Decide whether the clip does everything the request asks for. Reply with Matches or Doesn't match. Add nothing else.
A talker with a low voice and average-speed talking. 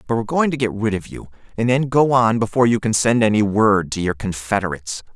Doesn't match